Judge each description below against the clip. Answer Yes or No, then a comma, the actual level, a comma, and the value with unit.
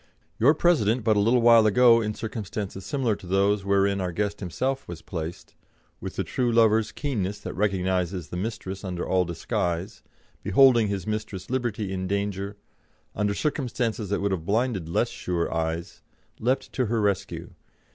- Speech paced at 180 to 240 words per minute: No, average, 165 wpm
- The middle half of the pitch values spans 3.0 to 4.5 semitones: Yes, average, 3.6 semitones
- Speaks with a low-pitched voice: Yes, low, 100 Hz